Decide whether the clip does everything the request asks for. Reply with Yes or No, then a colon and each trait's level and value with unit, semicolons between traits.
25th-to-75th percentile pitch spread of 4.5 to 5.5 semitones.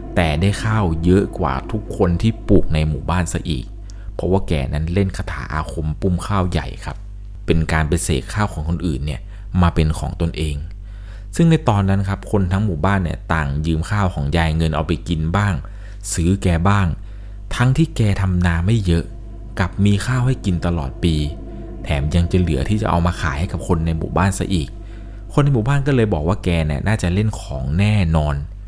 No: average, 3.7 semitones